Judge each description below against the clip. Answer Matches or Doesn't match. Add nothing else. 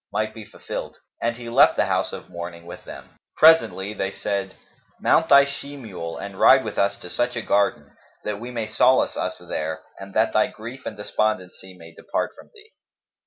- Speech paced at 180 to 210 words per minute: Matches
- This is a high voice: Doesn't match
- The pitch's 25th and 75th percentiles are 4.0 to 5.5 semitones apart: Matches